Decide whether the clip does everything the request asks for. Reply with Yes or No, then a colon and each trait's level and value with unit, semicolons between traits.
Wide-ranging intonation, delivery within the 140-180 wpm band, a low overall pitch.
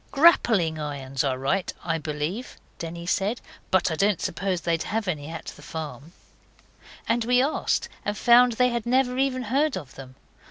No: wide, 7.4 semitones; average, 170 wpm; high, 190 Hz